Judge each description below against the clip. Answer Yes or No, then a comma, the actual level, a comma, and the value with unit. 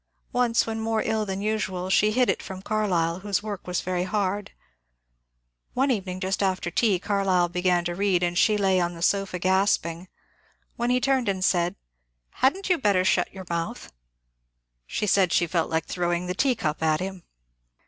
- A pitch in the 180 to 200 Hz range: Yes, high, 190 Hz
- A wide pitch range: No, average, 3.1 semitones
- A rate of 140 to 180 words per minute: No, average, 190 wpm